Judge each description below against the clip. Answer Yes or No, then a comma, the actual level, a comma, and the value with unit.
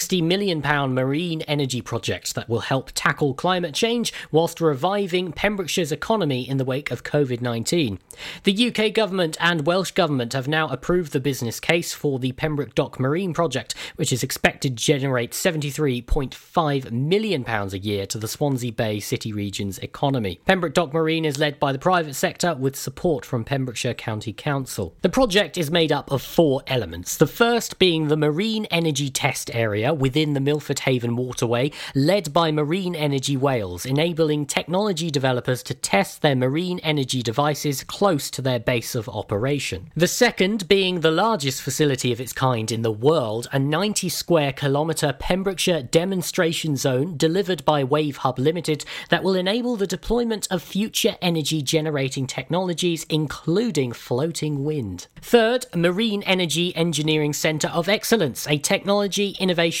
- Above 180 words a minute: No, average, 160 wpm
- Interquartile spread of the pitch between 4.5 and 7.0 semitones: Yes, average, 5.0 semitones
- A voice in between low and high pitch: Yes, medium, 150 Hz